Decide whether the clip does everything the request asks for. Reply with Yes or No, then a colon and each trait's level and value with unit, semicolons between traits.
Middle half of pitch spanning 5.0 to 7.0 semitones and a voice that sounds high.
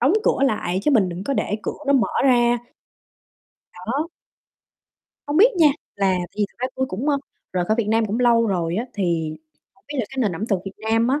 Yes: wide, 5.5 semitones; high, 225 Hz